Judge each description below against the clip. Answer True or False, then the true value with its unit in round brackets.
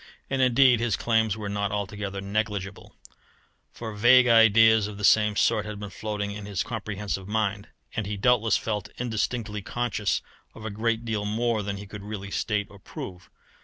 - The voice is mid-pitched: False (105 Hz)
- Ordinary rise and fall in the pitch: False (1.8 semitones)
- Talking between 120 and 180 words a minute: True (175 wpm)